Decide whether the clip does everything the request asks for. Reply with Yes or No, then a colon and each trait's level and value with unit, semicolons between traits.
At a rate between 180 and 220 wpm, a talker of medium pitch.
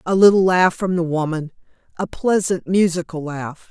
No: average, 145 wpm; medium, 175 Hz